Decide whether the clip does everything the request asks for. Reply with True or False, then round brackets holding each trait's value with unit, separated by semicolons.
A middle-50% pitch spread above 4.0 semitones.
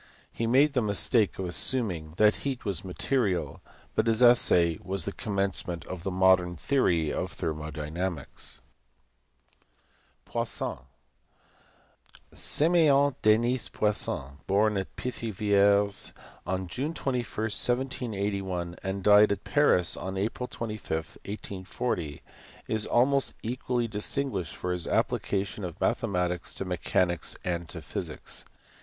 True (4.7 semitones)